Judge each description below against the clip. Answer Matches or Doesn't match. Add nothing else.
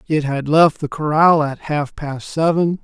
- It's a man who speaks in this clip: Matches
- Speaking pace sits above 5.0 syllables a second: Doesn't match